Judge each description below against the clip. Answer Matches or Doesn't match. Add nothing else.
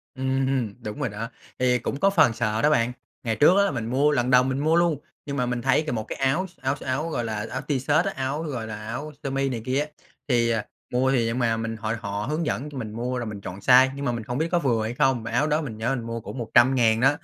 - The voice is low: Matches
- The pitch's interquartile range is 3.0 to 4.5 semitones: Matches